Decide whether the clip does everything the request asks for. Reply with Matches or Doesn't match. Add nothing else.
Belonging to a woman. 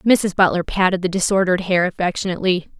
Matches